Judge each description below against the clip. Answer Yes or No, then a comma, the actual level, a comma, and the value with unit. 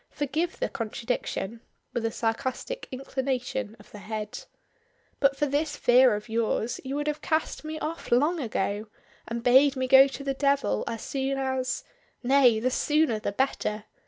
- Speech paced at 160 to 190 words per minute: Yes, average, 165 wpm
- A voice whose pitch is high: Yes, very high, 260 Hz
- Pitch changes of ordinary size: Yes, average, 3.6 semitones